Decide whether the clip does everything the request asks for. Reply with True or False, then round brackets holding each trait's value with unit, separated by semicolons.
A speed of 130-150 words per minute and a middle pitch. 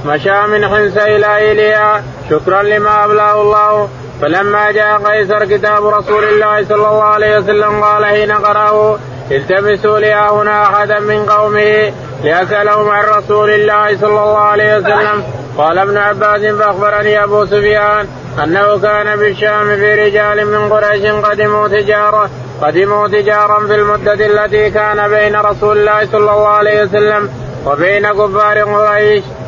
False (135 wpm; 210 Hz)